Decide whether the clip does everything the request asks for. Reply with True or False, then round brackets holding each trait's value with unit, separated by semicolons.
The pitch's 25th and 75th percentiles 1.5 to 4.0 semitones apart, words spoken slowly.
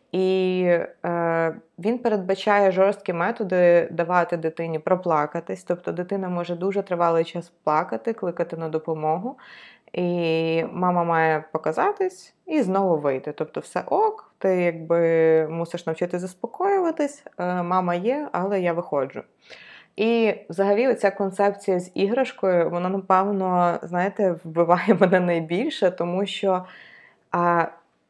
False (2.8 semitones; 115 wpm)